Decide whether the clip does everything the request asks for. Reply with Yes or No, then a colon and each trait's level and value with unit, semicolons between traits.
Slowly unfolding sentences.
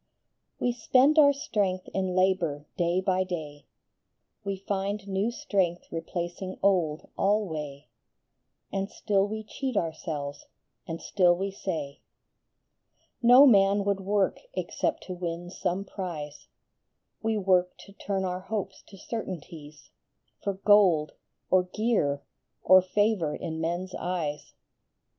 Yes: slow, 125 wpm